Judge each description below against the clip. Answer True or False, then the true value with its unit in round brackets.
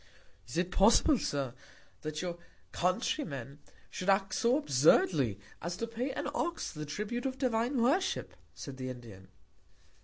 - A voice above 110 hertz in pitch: True (185 Hz)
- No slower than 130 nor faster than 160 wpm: True (150 wpm)